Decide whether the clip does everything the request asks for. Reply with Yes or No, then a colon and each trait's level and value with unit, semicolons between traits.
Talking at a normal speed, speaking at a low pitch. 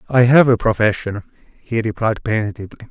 Yes: average, 145 wpm; low, 115 Hz